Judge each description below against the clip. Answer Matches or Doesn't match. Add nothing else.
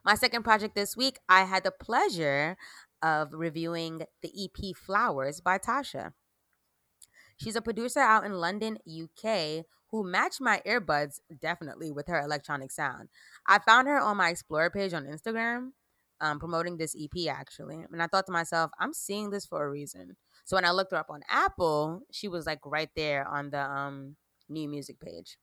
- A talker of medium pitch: Matches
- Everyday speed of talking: Matches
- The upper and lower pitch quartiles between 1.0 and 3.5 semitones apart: Doesn't match